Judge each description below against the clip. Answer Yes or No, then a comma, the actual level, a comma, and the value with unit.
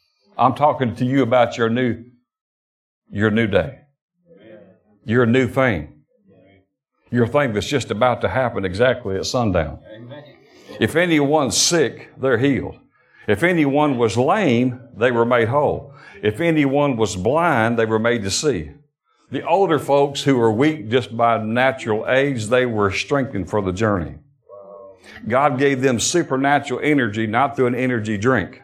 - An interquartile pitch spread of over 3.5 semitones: Yes, average, 4.2 semitones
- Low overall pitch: Yes, low, 120 Hz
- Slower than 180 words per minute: Yes, average, 150 wpm